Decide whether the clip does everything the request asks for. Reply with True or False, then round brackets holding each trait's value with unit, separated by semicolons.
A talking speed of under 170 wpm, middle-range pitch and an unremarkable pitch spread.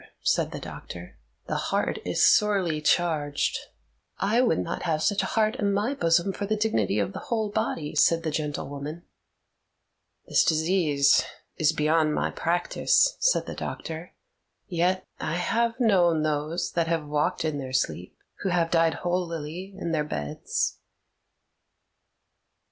True (145 wpm; 165 Hz; 4.6 semitones)